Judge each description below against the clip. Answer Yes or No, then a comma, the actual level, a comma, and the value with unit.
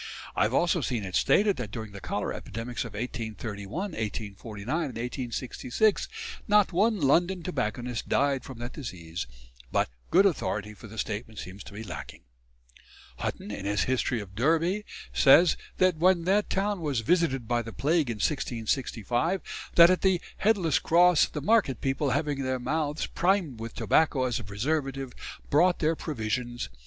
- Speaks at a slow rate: No, average, 160 wpm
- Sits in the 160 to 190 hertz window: No, low, 130 Hz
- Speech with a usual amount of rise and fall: No, wide, 7.2 semitones